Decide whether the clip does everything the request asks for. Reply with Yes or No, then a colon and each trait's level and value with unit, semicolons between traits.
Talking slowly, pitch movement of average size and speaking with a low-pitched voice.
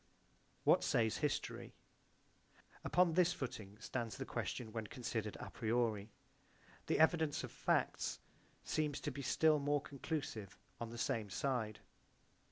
Yes: slow, 130 wpm; average, 5.0 semitones; low, 125 Hz